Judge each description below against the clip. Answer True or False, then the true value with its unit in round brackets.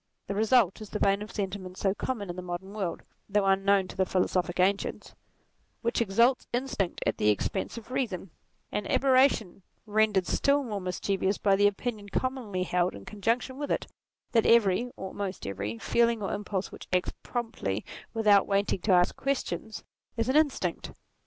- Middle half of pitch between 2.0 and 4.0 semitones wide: True (3.7 semitones)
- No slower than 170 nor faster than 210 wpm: True (180 wpm)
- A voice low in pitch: False (200 Hz)